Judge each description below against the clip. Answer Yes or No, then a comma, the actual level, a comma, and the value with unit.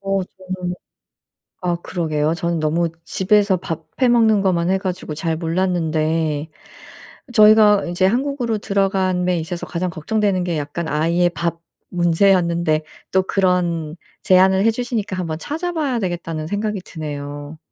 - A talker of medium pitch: Yes, medium, 180 Hz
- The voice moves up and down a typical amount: Yes, average, 3.1 semitones